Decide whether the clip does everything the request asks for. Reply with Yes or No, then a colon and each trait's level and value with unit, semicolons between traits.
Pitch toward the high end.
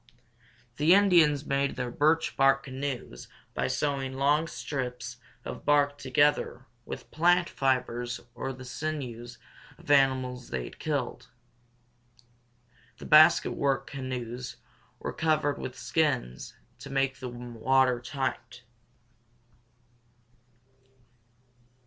No: low, 135 Hz